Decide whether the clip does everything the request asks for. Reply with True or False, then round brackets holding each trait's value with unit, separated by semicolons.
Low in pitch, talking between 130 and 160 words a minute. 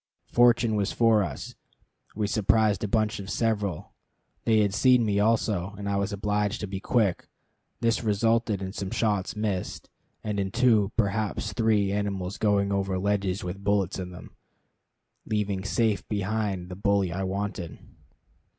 True (100 Hz; 155 wpm)